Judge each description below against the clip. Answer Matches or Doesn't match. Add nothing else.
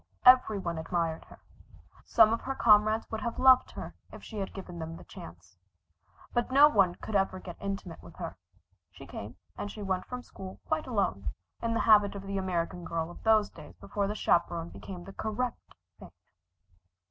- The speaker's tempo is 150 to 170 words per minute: Doesn't match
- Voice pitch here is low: Doesn't match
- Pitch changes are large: Doesn't match